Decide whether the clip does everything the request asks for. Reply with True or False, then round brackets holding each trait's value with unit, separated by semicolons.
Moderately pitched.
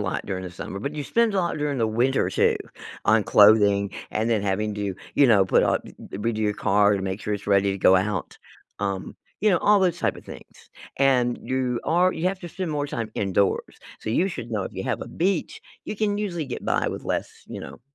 False (110 Hz)